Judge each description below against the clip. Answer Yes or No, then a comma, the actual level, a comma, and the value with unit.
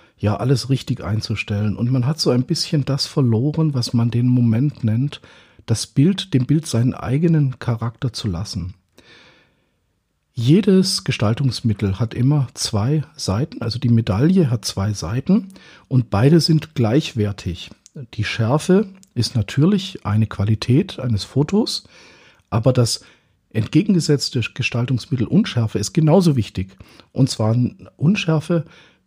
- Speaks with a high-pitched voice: No, low, 125 Hz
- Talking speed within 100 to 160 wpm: Yes, slow, 125 wpm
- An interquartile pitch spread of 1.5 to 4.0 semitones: No, wide, 5.6 semitones